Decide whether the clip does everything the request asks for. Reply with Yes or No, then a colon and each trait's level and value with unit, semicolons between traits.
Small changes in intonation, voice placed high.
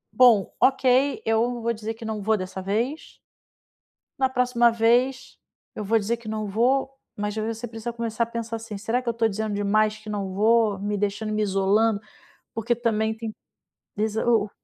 Yes: narrow, 1.9 semitones; high, 225 Hz